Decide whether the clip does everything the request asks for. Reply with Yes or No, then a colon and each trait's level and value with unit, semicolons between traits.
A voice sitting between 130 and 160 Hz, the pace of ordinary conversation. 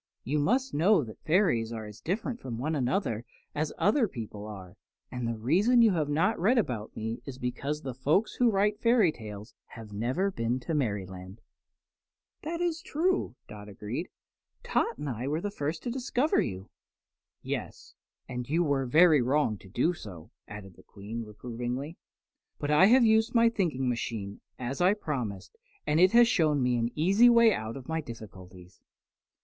Yes: medium, 140 Hz; average, 175 wpm